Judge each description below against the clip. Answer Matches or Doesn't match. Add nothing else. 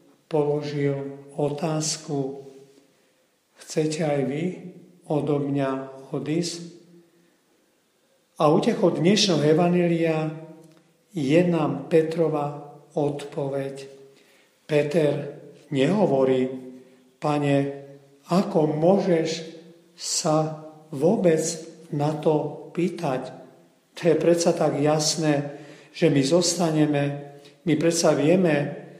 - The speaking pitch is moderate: Matches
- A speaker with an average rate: Doesn't match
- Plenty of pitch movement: Doesn't match